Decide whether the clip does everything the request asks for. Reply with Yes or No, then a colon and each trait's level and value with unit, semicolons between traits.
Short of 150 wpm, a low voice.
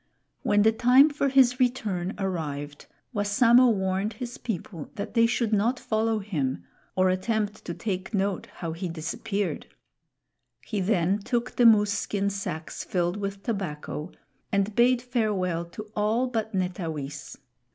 No: average, 140 wpm; high, 205 Hz